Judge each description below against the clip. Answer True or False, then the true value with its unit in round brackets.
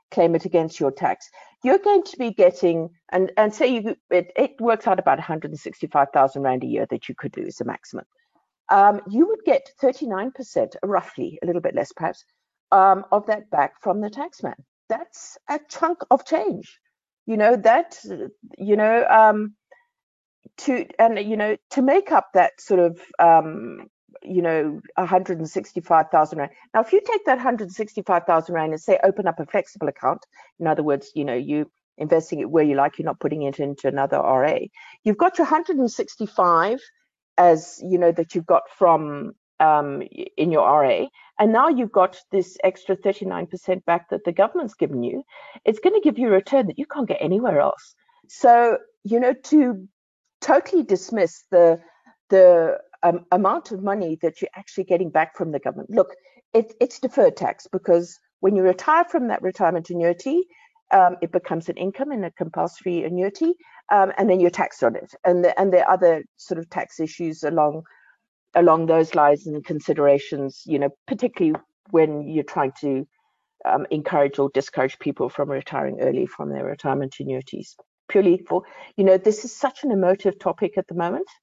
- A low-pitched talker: False (185 Hz)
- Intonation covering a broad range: True (7.0 semitones)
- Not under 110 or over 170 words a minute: False (185 wpm)